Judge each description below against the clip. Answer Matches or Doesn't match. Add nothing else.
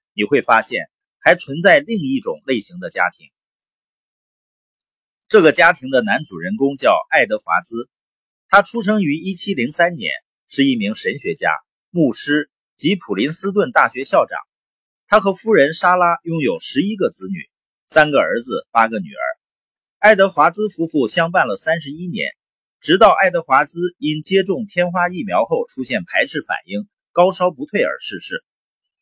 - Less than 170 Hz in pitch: Doesn't match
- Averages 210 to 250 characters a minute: Matches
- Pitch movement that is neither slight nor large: Doesn't match